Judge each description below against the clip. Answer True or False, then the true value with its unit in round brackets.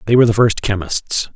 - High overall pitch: False (110 Hz)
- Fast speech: True (220 wpm)